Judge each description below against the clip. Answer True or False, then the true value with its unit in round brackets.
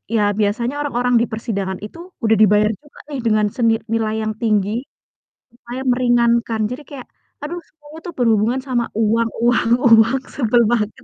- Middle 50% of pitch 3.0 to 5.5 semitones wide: False (2.5 semitones)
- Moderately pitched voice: False (235 Hz)